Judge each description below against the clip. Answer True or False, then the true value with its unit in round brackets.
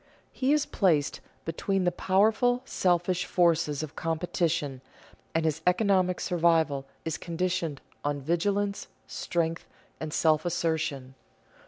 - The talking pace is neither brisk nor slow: False (115 wpm)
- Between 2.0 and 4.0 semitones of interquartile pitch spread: True (2.7 semitones)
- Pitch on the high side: False (170 Hz)